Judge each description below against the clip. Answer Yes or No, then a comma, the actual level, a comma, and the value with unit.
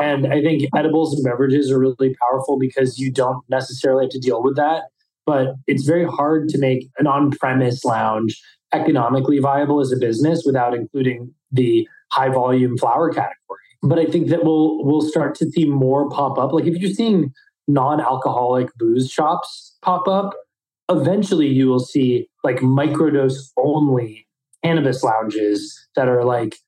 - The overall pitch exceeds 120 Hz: Yes, low, 135 Hz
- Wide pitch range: No, average, 3.3 semitones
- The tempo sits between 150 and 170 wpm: Yes, average, 160 wpm